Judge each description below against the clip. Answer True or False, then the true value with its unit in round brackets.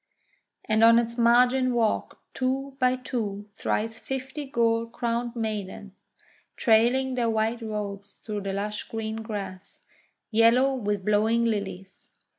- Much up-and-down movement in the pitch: False (2.7 semitones)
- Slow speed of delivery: True (125 wpm)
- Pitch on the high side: True (225 Hz)